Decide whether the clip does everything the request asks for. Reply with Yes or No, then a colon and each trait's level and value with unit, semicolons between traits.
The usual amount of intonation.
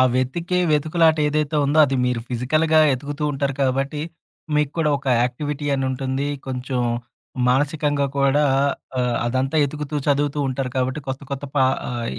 No: narrow, 2.3 semitones